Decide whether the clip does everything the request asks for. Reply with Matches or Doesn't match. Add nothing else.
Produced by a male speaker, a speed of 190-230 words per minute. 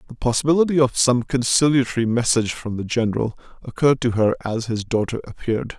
Doesn't match